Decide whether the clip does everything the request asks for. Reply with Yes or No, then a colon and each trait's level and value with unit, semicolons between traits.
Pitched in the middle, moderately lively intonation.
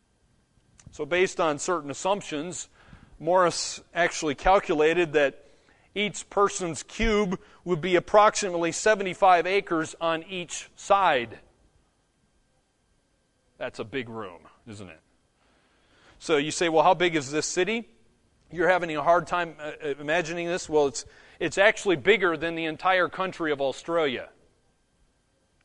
Yes: medium, 170 Hz; average, 3.3 semitones